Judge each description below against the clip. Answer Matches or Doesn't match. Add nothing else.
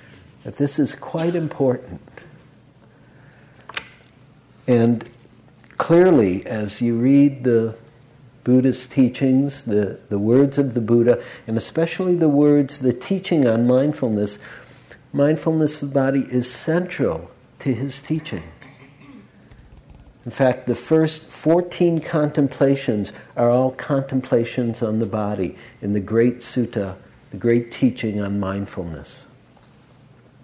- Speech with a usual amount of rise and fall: Matches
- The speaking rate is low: Matches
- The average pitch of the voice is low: Matches